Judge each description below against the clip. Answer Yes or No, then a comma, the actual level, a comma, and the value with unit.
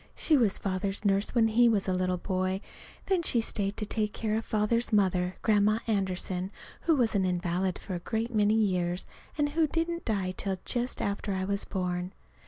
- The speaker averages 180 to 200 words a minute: Yes, average, 190 wpm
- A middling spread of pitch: Yes, average, 3.3 semitones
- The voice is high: Yes, high, 200 Hz